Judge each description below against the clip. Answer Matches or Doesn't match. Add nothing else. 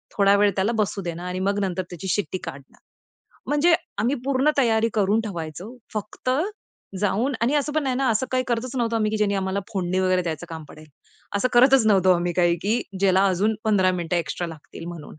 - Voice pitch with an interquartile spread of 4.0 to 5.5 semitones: Matches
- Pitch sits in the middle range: Doesn't match